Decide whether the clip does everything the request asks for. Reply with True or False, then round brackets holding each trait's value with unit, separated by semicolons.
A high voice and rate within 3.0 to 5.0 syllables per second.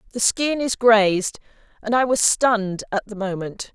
True (220 Hz; 4.7 syllables/s)